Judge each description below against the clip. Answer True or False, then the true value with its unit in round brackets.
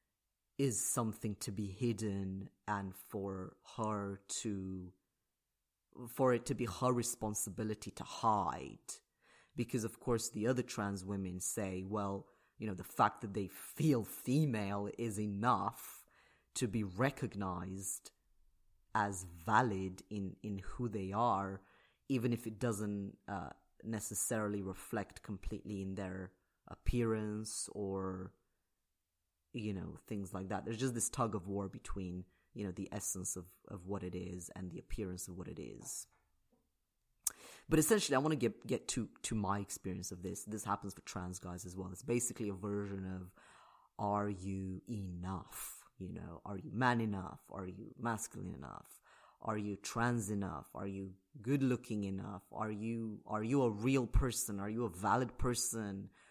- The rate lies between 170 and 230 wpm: False (155 wpm)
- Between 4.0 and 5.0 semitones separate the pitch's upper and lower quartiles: False (3.2 semitones)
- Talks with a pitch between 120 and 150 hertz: False (100 Hz)